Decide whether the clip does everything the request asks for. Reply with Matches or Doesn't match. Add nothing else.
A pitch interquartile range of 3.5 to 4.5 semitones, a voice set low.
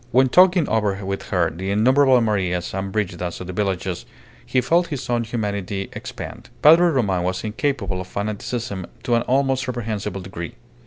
Doesn't match